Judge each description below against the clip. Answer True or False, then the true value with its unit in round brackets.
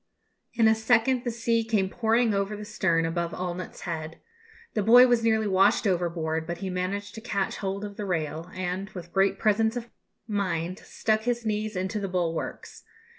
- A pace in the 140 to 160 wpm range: False (180 wpm)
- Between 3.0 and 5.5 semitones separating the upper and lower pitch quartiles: True (3.6 semitones)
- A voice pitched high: True (200 Hz)